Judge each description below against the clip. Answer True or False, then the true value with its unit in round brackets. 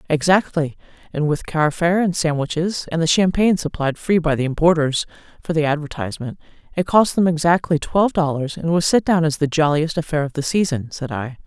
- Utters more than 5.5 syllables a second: True (5.7 syllables/s)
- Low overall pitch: False (160 Hz)